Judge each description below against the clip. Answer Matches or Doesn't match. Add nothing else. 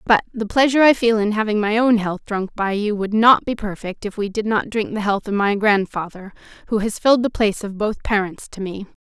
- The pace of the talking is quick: Matches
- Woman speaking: Matches